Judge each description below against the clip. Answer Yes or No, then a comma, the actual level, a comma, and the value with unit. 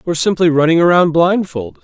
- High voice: No, medium, 165 Hz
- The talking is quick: No, average, 165 wpm